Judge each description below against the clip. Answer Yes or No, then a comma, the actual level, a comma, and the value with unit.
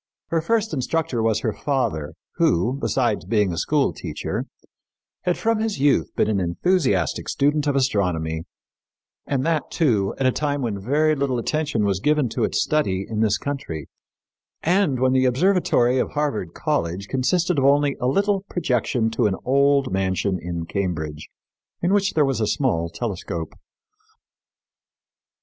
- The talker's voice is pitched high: No, low, 130 Hz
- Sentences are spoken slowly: No, average, 155 wpm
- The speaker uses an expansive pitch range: Yes, wide, 7.2 semitones